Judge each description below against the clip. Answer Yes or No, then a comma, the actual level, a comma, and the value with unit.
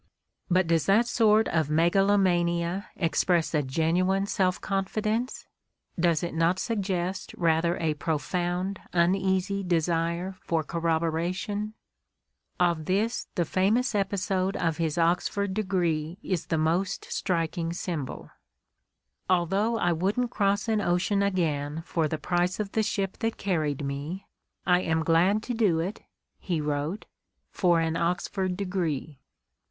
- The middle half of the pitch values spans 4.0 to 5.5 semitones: No, average, 3.2 semitones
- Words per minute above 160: No, slow, 135 wpm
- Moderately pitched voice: Yes, medium, 180 Hz